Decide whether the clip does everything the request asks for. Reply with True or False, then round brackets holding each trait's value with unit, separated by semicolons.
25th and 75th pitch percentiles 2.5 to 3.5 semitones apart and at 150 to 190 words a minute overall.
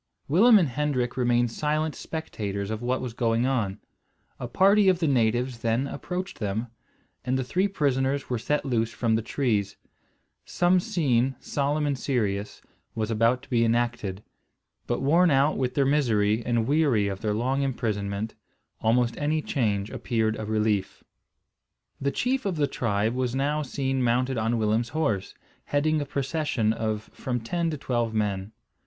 False (4.5 semitones; 160 wpm)